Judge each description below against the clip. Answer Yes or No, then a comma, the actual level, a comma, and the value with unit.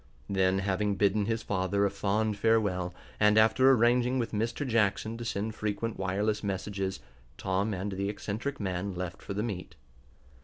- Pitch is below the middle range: Yes, low, 105 Hz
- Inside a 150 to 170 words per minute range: Yes, average, 160 wpm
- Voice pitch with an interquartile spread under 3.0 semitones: Yes, narrow, 2.5 semitones